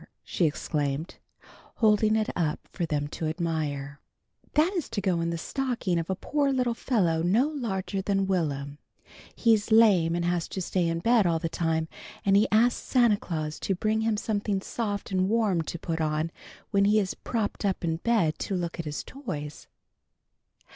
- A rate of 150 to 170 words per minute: No, average, 180 wpm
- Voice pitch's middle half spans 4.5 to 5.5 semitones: Yes, average, 5.0 semitones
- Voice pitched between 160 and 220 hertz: Yes, high, 190 Hz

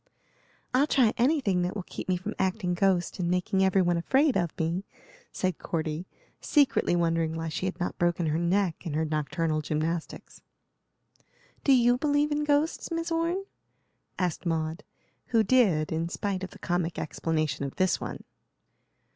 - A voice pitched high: No, medium, 180 Hz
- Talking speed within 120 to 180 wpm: Yes, average, 165 wpm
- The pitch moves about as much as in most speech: No, wide, 6.2 semitones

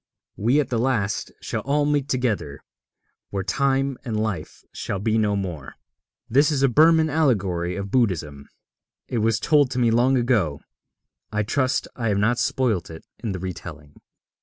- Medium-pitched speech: No, low, 115 Hz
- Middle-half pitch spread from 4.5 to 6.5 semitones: Yes, wide, 5.6 semitones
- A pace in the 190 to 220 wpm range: No, average, 160 wpm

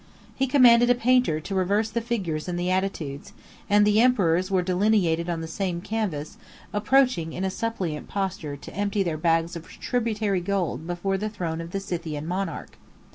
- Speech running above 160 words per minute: Yes, average, 180 wpm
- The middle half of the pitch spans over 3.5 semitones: Yes, average, 4.2 semitones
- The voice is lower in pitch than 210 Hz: Yes, high, 190 Hz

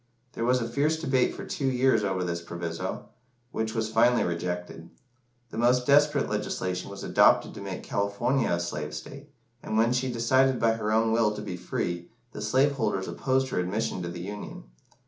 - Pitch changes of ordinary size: No, wide, 5.9 semitones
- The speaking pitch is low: Yes, low, 110 Hz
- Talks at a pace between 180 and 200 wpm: Yes, average, 185 wpm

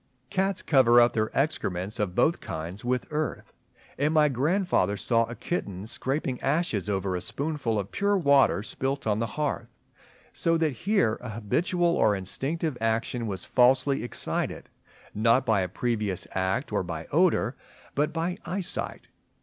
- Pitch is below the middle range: Yes, low, 125 Hz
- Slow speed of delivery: No, average, 155 wpm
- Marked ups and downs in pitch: Yes, wide, 6.6 semitones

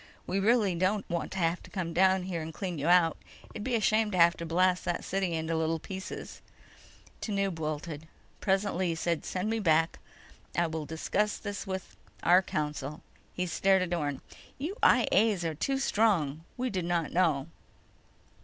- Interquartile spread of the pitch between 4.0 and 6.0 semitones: No, average, 3.1 semitones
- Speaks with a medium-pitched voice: Yes, medium, 180 Hz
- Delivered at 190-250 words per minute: No, average, 180 wpm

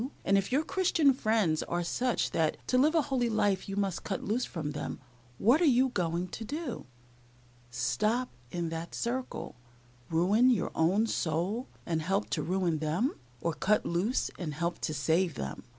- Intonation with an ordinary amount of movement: No, wide, 6.6 semitones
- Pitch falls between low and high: No, high, 195 Hz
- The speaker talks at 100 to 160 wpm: No, average, 175 wpm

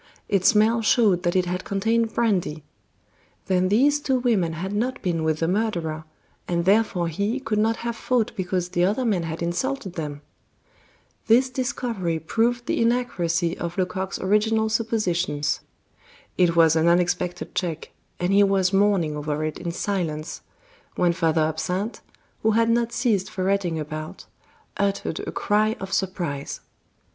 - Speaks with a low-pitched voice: No, high, 190 Hz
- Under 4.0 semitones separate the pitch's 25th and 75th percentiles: No, average, 4.6 semitones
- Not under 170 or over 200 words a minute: No, average, 150 wpm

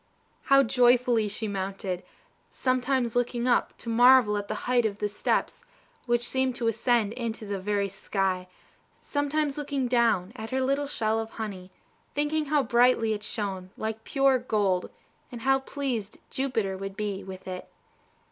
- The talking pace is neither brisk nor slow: Yes, average, 155 wpm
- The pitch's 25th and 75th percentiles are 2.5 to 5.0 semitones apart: Yes, average, 4.0 semitones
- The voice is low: No, high, 230 Hz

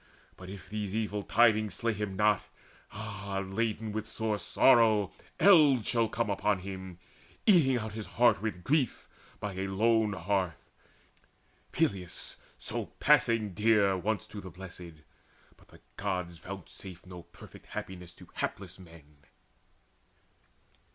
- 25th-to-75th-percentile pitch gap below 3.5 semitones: Yes, average, 2.8 semitones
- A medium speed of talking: No, slow, 130 wpm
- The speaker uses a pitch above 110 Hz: No, low, 100 Hz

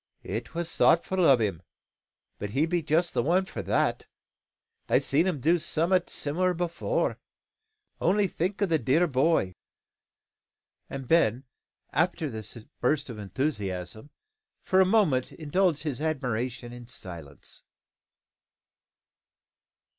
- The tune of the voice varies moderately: No, wide, 6.3 semitones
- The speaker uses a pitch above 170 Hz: No, medium, 150 Hz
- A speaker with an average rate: No, slow, 125 wpm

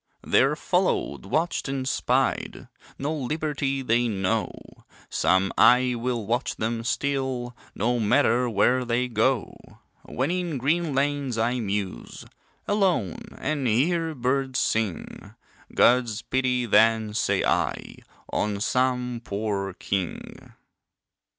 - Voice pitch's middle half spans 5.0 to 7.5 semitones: No, average, 3.5 semitones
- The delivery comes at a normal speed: No, slow, 110 wpm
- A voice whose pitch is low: Yes, low, 125 Hz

